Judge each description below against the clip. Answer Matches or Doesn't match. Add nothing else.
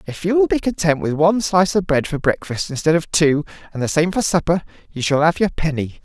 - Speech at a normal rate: Doesn't match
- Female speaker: Doesn't match